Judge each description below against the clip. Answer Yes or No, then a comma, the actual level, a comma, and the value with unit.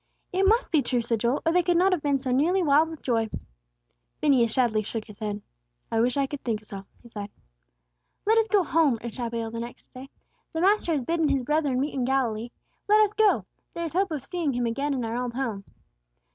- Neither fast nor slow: No, fast, 230 wpm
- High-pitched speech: Yes, very high, 270 Hz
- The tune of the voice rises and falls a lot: Yes, wide, 5.9 semitones